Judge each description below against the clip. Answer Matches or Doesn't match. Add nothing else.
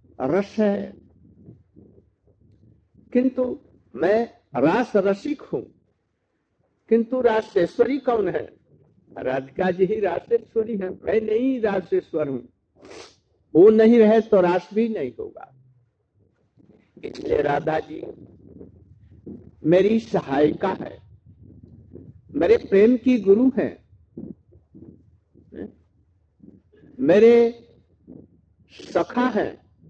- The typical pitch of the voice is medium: Doesn't match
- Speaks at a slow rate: Matches